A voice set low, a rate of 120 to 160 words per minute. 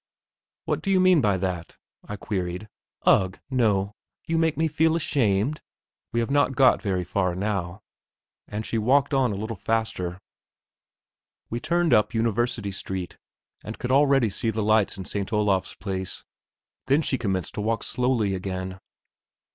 Yes: low, 110 Hz; average, 155 wpm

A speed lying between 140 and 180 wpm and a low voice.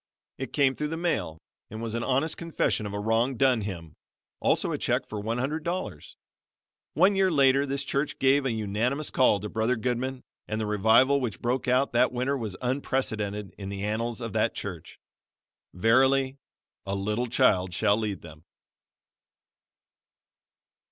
Yes: average, 165 wpm; low, 120 Hz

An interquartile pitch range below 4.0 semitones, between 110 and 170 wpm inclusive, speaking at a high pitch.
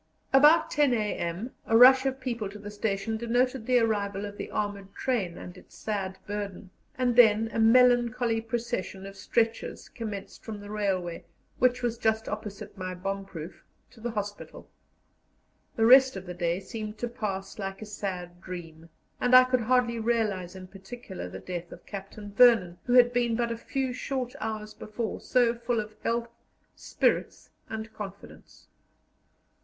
Yes: average, 3.5 semitones; average, 165 wpm; high, 220 Hz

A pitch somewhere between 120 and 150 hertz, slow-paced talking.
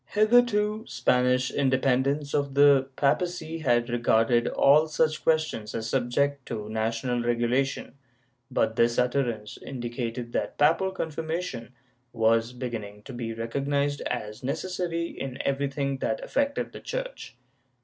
Yes: low, 135 Hz; slow, 125 wpm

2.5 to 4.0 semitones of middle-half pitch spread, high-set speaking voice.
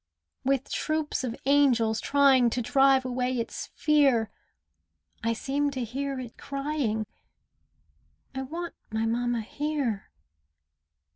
Yes: average, 3.4 semitones; very high, 260 Hz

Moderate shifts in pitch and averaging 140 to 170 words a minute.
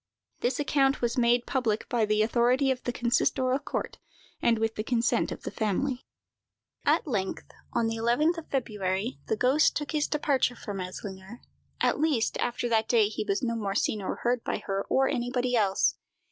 No: average, 3.4 semitones; average, 185 wpm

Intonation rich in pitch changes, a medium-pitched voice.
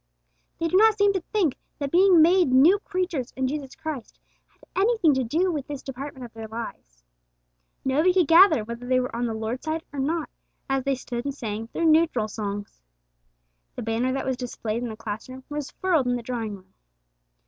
No: wide, 5.8 semitones; very high, 265 Hz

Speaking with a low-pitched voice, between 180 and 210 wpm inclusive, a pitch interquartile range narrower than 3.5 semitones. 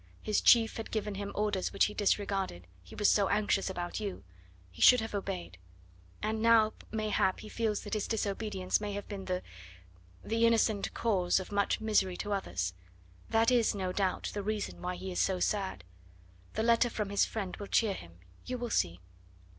No: high, 205 Hz; average, 185 wpm; narrow, 2.6 semitones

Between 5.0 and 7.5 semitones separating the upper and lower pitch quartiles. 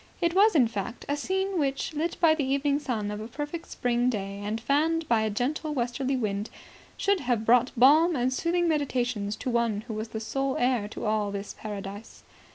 Yes: wide, 5.4 semitones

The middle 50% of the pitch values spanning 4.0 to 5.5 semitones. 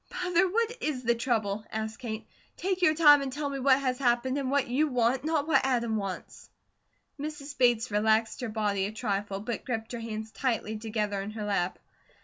Yes: average, 4.4 semitones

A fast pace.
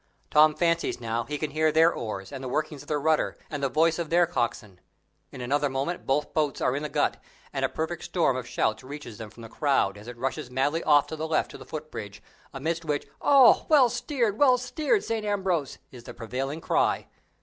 Yes: fast, 220 wpm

